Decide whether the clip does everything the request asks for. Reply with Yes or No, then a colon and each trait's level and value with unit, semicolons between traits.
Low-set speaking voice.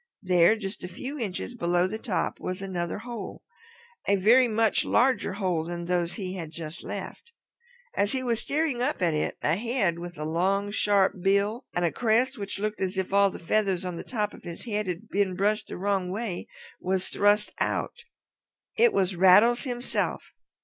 No: high, 200 Hz